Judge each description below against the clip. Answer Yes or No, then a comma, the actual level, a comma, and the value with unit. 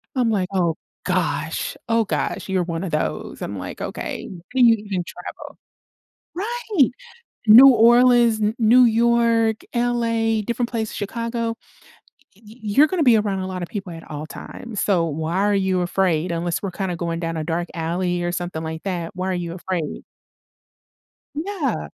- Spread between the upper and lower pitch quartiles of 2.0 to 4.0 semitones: No, average, 5.0 semitones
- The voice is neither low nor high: No, high, 205 Hz